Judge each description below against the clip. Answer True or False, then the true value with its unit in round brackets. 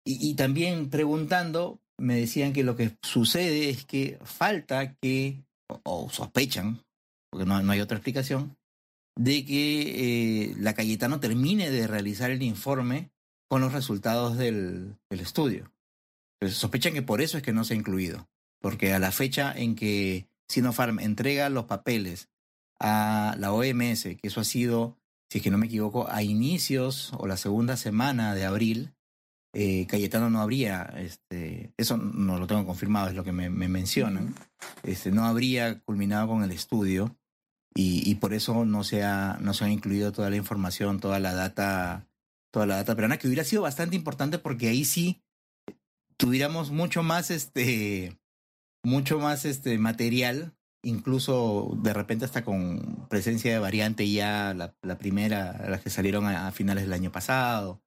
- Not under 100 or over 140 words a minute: False (170 wpm)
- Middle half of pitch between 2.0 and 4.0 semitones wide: False (4.7 semitones)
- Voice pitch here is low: True (110 Hz)